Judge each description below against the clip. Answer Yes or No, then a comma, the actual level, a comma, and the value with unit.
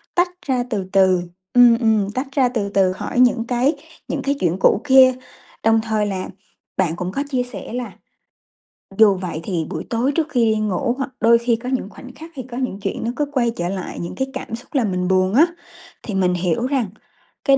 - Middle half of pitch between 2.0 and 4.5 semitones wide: No, average, 5.1 semitones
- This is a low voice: No, high, 230 Hz